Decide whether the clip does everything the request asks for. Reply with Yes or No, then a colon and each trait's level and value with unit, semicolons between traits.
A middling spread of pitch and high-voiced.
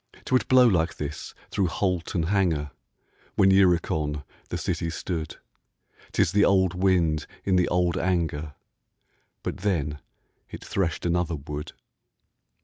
No: average, 3.4 semitones; very low, 85 Hz